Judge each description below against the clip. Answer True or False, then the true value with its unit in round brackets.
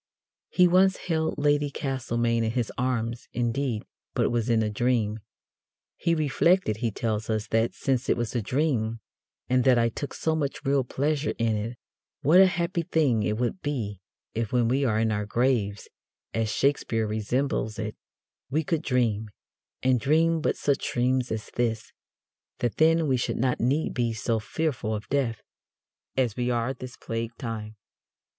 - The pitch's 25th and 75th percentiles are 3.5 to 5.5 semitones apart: True (4.1 semitones)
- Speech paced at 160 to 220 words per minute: True (175 wpm)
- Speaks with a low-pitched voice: True (120 Hz)